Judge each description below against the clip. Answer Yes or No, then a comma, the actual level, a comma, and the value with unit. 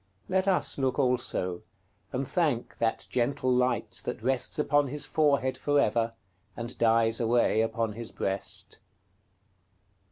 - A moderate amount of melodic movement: Yes, average, 3.7 semitones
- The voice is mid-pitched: No, low, 125 Hz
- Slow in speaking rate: Yes, slow, 130 wpm